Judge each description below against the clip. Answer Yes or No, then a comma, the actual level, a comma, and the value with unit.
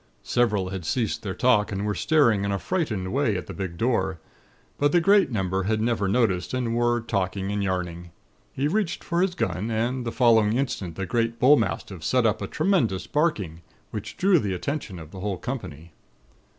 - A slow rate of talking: No, average, 190 wpm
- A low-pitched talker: Yes, low, 110 Hz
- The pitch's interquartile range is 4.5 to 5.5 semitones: Yes, average, 5.2 semitones